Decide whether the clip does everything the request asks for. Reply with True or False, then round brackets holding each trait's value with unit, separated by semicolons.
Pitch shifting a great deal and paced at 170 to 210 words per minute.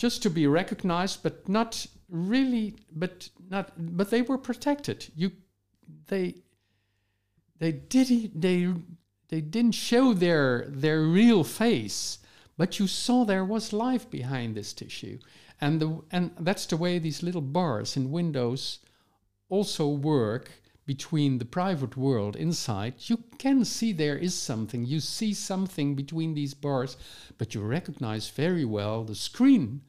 False (7.1 semitones; 145 wpm)